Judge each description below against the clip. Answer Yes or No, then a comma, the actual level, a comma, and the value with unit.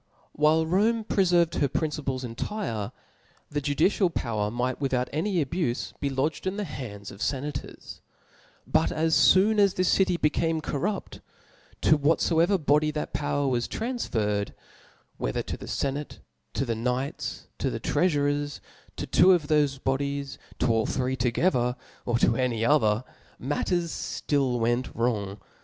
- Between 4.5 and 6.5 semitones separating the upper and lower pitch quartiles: Yes, average, 5.0 semitones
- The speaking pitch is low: No, medium, 145 Hz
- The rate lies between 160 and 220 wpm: No, average, 145 wpm